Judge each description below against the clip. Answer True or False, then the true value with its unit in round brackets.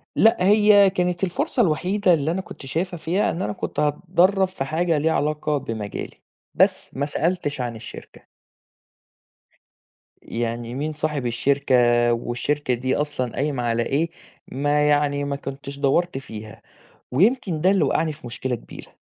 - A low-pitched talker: False (150 Hz)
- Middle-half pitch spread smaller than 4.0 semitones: False (5.2 semitones)